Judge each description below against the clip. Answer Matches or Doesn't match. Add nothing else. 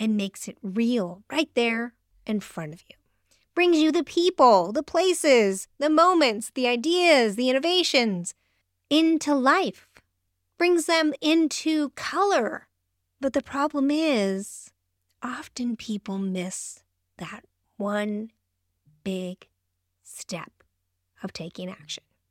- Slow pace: Matches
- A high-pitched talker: Matches